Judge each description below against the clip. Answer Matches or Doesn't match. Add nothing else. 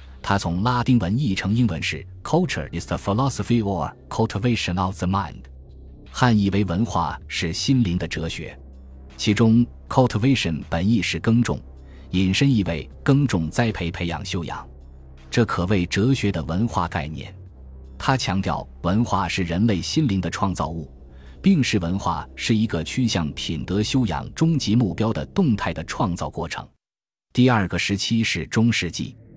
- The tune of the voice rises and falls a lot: Matches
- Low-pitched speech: Matches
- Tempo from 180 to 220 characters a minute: Doesn't match